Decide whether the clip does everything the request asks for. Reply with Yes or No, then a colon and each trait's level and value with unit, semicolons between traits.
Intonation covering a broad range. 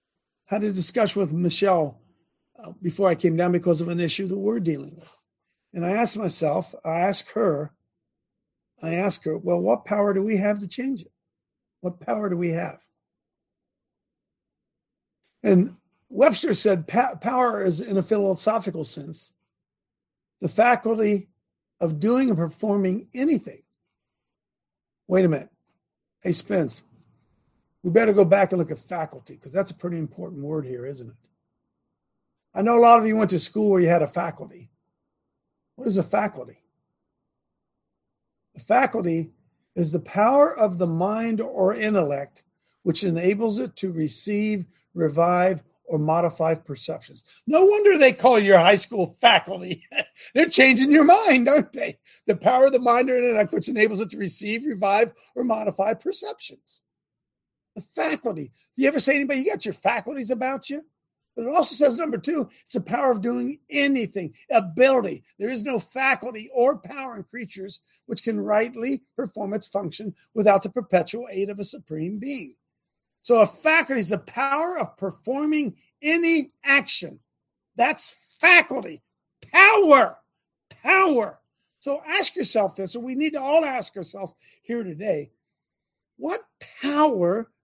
Yes: wide, 6.2 semitones